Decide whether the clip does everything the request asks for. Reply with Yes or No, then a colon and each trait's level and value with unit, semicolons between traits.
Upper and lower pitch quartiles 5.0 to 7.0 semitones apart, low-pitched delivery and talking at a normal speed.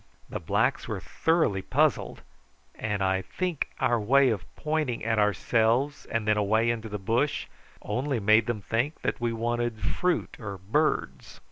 No: average, 4.2 semitones; low, 115 Hz; average, 155 wpm